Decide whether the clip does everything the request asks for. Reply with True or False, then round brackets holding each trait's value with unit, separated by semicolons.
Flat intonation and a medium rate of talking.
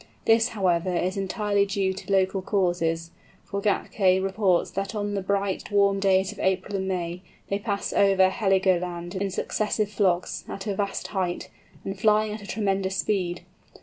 True (1.4 semitones; 165 wpm)